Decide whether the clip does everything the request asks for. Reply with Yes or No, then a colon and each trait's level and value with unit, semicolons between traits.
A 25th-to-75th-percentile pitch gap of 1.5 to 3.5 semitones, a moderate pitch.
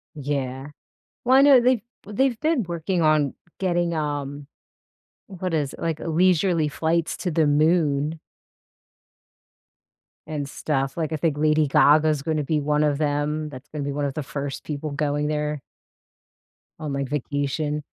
Yes: narrow, 2.4 semitones; medium, 150 Hz